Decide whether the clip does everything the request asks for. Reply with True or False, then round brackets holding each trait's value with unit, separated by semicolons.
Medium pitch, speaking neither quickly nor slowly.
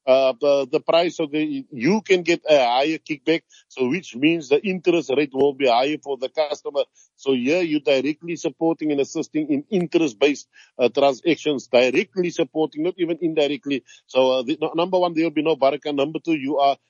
True (155 Hz; 190 wpm)